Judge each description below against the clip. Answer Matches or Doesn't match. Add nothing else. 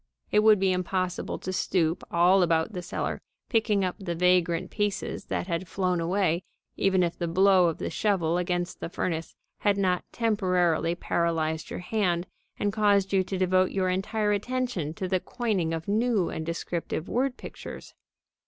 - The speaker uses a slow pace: Doesn't match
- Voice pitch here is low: Doesn't match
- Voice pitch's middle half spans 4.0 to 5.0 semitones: Doesn't match